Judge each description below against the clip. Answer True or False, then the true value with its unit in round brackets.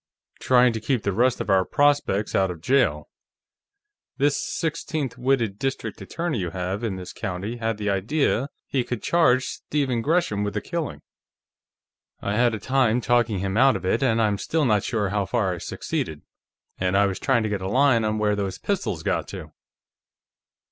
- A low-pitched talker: True (115 Hz)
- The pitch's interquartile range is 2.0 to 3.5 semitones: False (4.9 semitones)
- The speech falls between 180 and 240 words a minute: True (185 wpm)